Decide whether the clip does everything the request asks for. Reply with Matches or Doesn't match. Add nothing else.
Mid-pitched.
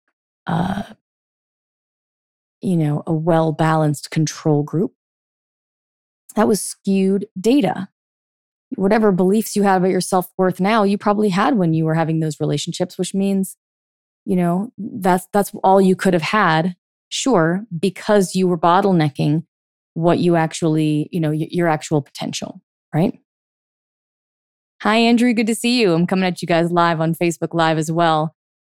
Matches